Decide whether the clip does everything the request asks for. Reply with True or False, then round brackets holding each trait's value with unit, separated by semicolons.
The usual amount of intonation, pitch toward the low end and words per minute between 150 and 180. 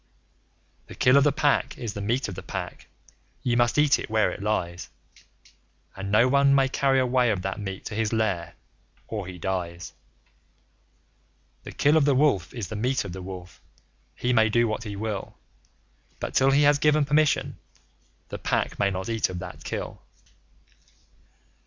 False (5.7 semitones; 110 Hz; 175 wpm)